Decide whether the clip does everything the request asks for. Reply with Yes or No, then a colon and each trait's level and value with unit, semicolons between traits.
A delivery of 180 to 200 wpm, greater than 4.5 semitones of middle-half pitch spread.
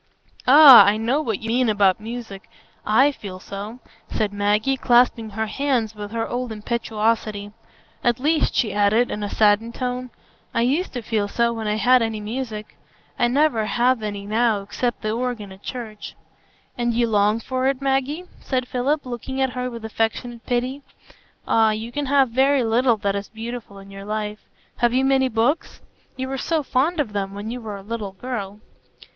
No: average, 185 wpm; average, 3.2 semitones